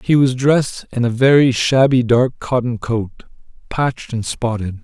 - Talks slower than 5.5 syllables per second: Yes, 4.5 syllables/s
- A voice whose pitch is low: Yes, low, 125 Hz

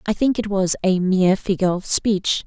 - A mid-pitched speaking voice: No, high, 195 Hz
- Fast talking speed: Yes, fast, 220 wpm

